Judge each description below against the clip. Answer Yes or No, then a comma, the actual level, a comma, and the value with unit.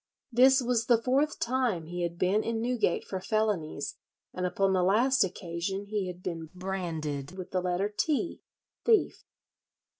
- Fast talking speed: No, average, 155 wpm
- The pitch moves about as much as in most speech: Yes, average, 4.9 semitones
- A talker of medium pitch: No, high, 195 Hz